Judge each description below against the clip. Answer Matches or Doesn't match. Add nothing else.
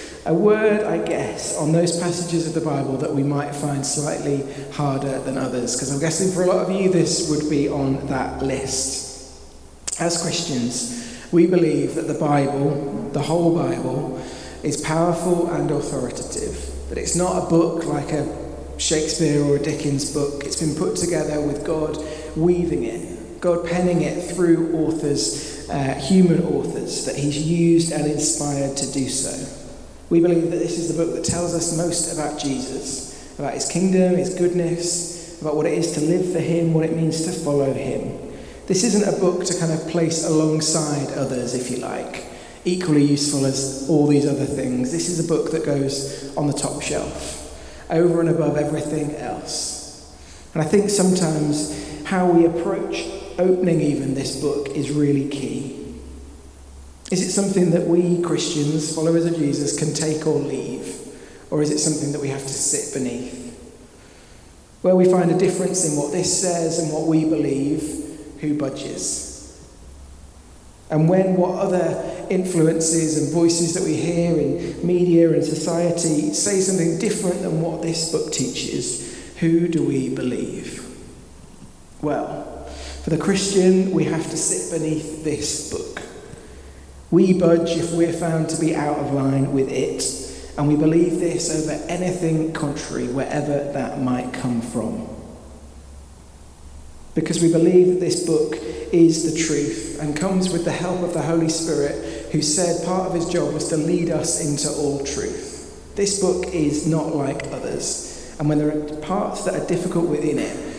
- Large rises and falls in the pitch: Doesn't match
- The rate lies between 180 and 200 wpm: Doesn't match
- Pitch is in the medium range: Matches